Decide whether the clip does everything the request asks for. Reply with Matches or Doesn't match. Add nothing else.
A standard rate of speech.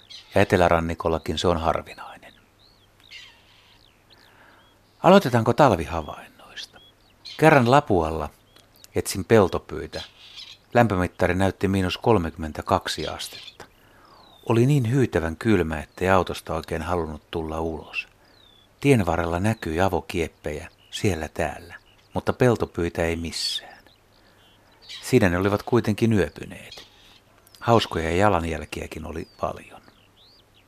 Doesn't match